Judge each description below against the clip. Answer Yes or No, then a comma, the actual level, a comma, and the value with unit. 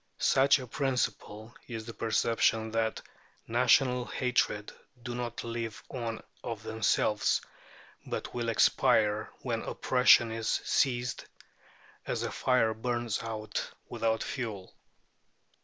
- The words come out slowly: Yes, slow, 110 wpm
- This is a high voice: No, low, 115 Hz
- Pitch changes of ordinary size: No, narrow, 1.9 semitones